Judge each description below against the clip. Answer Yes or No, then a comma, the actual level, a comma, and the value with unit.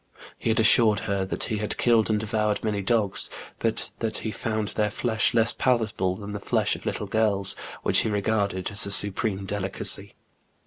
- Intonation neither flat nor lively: No, narrow, 1.8 semitones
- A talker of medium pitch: No, low, 105 Hz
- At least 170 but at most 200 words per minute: Yes, average, 185 wpm